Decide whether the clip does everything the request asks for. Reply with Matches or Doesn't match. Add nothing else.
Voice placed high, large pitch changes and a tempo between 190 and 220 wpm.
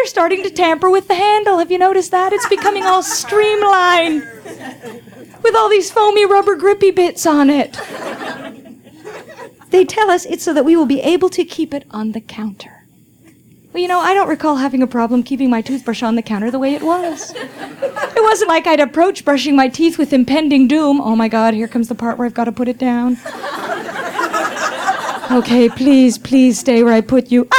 Matches